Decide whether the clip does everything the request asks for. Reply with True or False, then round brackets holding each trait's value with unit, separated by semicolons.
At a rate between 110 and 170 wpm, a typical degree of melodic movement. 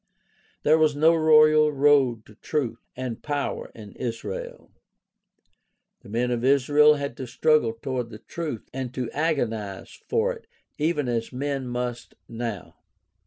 True (140 wpm; 4.4 semitones)